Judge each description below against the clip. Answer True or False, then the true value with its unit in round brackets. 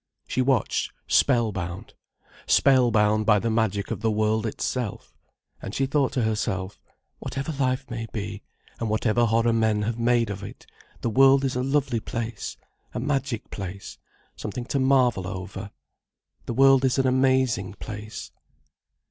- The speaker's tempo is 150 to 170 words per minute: True (155 wpm)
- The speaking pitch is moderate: False (115 Hz)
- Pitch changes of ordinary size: True (3.7 semitones)